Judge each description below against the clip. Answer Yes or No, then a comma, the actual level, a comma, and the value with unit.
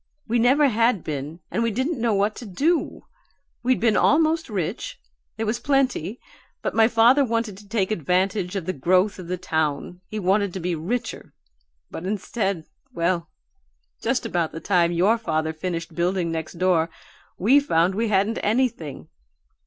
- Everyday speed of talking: Yes, average, 165 wpm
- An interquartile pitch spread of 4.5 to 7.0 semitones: Yes, average, 5.2 semitones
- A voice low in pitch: No, high, 195 Hz